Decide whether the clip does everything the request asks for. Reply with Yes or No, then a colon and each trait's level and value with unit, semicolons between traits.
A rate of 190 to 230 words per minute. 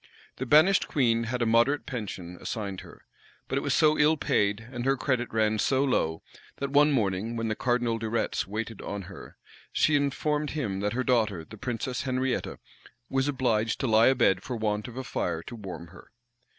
Yes: average, 195 wpm